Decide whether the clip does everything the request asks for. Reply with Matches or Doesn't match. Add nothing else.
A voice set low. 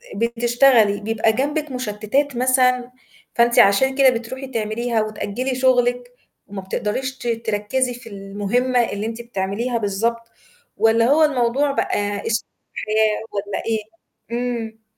Doesn't match